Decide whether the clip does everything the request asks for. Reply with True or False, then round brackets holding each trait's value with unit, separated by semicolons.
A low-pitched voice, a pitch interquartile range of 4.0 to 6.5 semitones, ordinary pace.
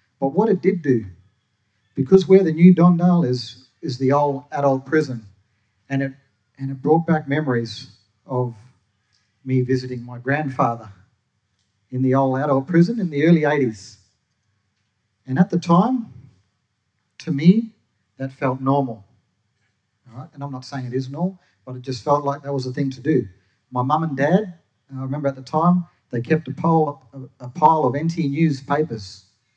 True (130 Hz; 5.3 semitones; 175 wpm)